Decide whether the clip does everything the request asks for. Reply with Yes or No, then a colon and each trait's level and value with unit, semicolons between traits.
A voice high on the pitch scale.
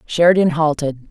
No: medium, 160 Hz